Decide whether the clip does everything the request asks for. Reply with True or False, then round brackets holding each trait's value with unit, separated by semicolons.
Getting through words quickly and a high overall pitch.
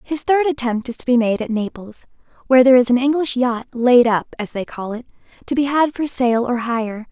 True (235 wpm; 250 Hz)